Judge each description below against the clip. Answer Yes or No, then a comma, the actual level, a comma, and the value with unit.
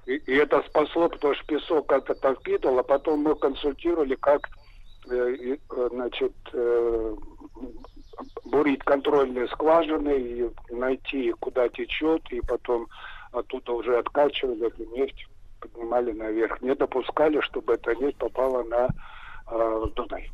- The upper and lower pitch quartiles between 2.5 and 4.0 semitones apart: No, average, 5.0 semitones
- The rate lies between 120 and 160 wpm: No, slow, 110 wpm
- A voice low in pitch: Yes, low, 130 Hz